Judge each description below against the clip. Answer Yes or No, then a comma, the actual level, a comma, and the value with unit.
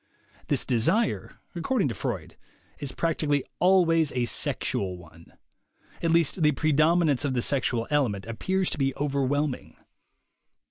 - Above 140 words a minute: No, slow, 135 wpm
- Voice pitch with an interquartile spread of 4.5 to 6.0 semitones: Yes, average, 5.0 semitones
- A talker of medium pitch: Yes, medium, 145 Hz